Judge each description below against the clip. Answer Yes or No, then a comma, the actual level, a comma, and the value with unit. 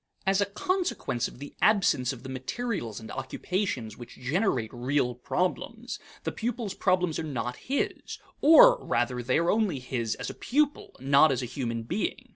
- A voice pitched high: No, medium, 145 Hz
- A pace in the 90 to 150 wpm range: No, average, 170 wpm